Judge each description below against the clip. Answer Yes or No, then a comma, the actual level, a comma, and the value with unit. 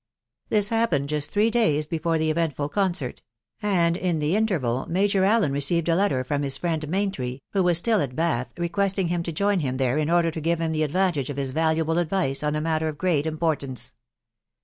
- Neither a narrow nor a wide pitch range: Yes, average, 4.2 semitones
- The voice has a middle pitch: Yes, medium, 165 Hz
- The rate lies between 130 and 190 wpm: No, fast, 205 wpm